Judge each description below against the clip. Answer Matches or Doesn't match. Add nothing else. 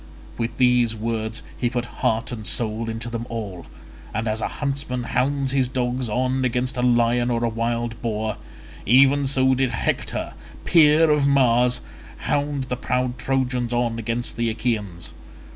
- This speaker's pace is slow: Doesn't match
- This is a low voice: Matches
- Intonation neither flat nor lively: Doesn't match